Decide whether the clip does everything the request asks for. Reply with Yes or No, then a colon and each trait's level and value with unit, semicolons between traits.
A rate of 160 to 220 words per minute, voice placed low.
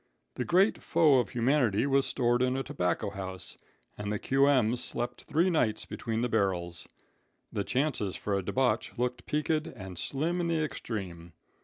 Yes: average, 165 wpm; low, 120 Hz